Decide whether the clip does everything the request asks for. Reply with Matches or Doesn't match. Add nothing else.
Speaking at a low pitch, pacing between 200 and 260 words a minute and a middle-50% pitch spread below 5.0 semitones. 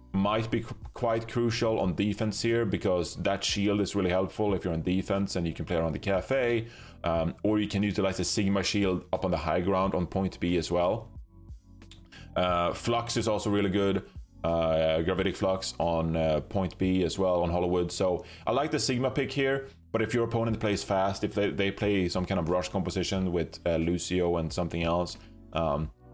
Matches